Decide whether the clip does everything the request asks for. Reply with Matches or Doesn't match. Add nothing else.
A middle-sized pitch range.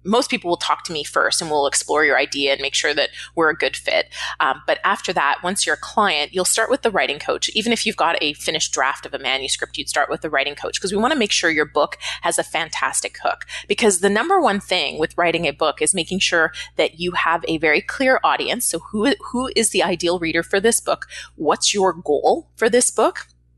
Doesn't match